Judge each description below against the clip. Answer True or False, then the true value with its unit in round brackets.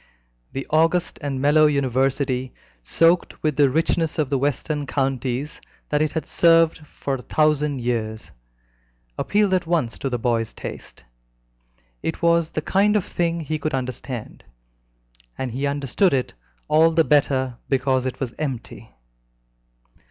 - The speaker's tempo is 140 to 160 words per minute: True (145 wpm)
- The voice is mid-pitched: True (145 Hz)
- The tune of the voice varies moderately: True (3.6 semitones)